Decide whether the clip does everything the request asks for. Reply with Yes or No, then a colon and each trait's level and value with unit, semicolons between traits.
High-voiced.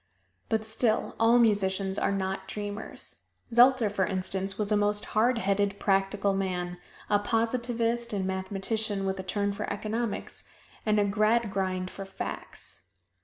Yes: high, 205 Hz